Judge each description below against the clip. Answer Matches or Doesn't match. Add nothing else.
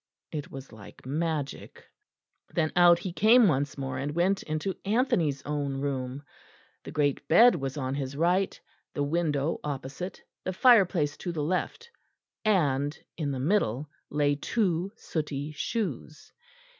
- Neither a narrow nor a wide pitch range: Matches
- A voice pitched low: Doesn't match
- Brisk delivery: Doesn't match